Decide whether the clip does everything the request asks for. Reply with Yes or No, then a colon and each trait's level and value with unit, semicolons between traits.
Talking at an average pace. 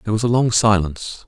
No: fast, 235 wpm